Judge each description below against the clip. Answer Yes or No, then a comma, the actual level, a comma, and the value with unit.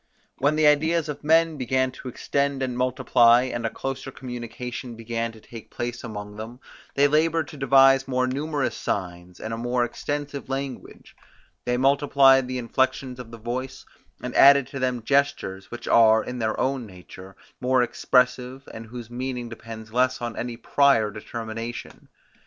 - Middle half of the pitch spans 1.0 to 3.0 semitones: Yes, average, 2.7 semitones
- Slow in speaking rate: No, average, 165 wpm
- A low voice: Yes, low, 125 Hz